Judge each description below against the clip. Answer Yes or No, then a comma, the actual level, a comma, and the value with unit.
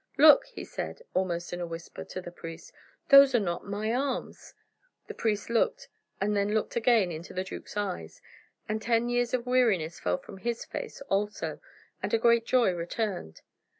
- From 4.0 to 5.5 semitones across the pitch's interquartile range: Yes, average, 5.2 semitones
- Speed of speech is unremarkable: Yes, average, 180 wpm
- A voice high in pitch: Yes, high, 210 Hz